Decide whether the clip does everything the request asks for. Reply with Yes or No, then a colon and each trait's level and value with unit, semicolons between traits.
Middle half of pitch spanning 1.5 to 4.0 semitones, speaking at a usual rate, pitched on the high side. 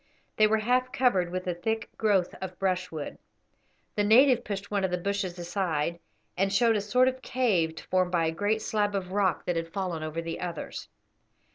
Yes: average, 3.5 semitones; average, 190 wpm; high, 195 Hz